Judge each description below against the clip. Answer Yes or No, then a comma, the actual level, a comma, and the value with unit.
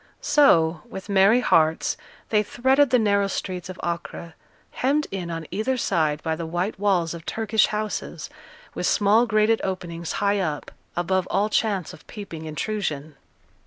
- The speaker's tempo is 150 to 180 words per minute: Yes, average, 155 wpm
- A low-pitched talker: No, high, 195 Hz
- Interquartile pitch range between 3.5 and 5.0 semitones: Yes, average, 4.3 semitones